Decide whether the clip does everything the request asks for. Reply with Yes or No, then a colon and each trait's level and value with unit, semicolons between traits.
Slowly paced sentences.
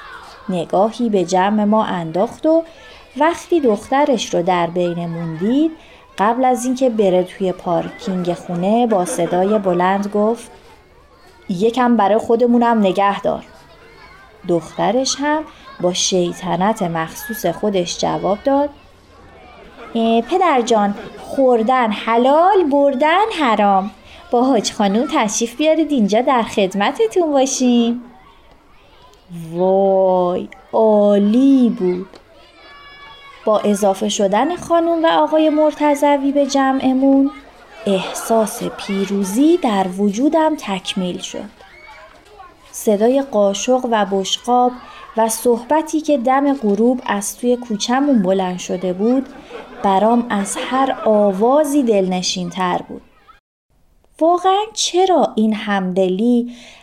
Yes: slow, 100 wpm